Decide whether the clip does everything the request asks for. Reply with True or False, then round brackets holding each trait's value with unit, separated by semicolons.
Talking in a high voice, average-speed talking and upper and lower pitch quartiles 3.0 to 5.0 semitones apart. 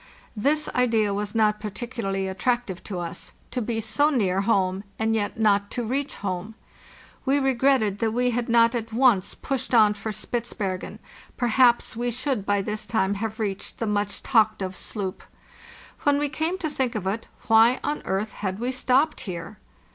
True (220 Hz; 175 wpm; 3.5 semitones)